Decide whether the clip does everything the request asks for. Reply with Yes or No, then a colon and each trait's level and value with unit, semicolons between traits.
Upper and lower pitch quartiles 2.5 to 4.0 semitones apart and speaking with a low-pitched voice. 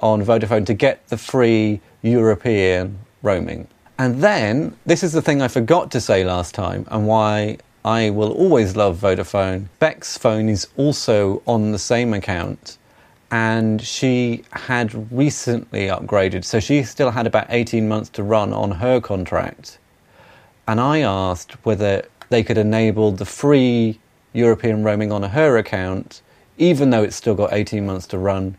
Yes: average, 2.8 semitones; low, 110 Hz